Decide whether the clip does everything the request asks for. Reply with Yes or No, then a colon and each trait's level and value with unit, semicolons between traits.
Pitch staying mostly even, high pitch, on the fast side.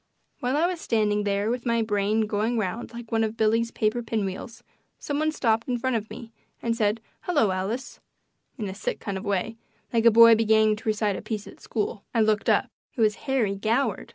Yes: narrow, 1.9 semitones; high, 220 Hz; fast, 215 wpm